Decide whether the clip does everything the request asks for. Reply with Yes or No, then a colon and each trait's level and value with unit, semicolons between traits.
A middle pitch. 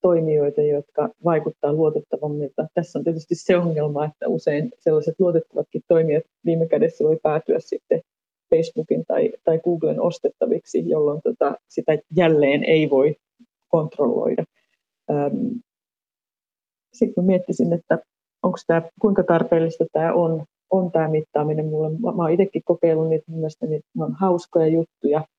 Yes: medium, 165 Hz